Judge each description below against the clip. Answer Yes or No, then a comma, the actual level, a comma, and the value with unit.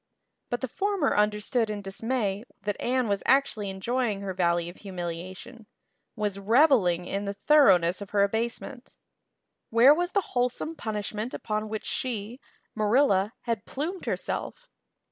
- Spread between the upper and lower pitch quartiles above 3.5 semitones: Yes, average, 4.2 semitones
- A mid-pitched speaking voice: No, high, 215 Hz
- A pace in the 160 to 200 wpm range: No, average, 145 wpm